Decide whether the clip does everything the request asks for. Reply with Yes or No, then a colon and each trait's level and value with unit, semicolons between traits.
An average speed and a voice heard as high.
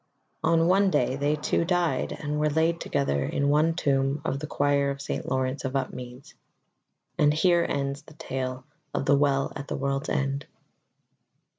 No: average, 170 wpm; medium, 140 Hz